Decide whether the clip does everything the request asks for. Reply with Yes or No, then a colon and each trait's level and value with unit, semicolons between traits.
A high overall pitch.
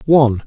No: low, 130 Hz